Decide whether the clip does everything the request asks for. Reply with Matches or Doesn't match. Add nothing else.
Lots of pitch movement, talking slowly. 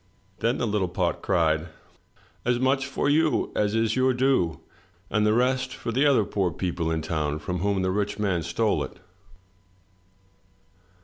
Doesn't match